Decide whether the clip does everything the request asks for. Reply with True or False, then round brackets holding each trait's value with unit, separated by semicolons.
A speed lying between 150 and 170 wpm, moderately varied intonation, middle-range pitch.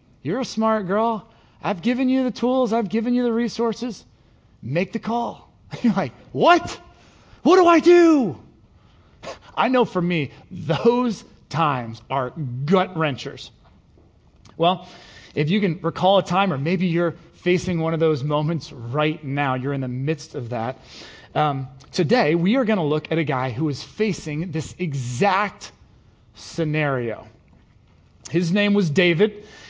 False (155 wpm; 7.7 semitones; 165 Hz)